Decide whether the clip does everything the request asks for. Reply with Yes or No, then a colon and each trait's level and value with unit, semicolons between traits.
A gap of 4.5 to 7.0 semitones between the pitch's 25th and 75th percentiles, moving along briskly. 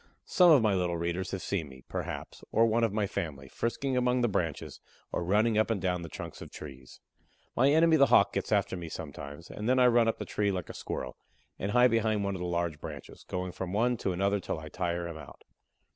Yes: average, 5.1 semitones; fast, 235 wpm